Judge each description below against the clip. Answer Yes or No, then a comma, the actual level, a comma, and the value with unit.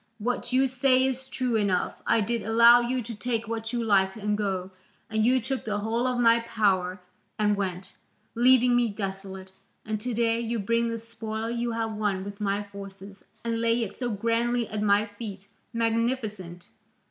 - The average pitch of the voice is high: Yes, high, 225 Hz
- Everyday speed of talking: Yes, average, 180 wpm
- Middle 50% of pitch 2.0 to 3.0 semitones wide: Yes, average, 2.7 semitones